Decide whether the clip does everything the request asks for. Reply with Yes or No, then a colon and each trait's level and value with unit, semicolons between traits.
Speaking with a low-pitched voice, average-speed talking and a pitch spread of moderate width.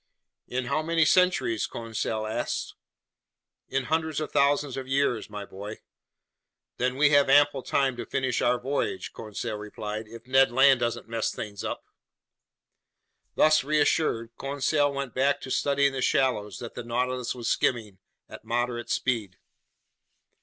Yes: low, 130 Hz; average, 145 wpm; average, 3.6 semitones